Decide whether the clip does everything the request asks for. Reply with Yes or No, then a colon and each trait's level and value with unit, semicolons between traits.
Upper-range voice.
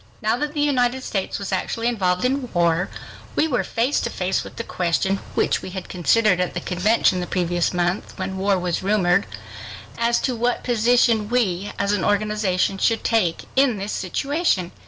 Yes: high, 205 Hz